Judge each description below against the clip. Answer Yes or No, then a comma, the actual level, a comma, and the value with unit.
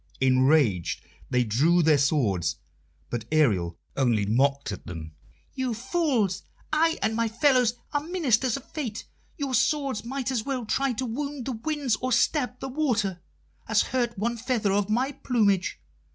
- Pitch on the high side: Yes, high, 225 Hz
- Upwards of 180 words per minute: No, average, 155 wpm